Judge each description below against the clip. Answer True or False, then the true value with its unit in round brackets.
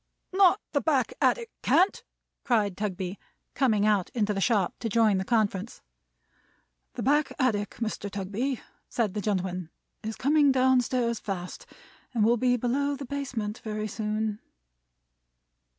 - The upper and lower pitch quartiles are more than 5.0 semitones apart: False (4.1 semitones)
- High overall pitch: True (220 Hz)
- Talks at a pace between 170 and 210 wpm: False (140 wpm)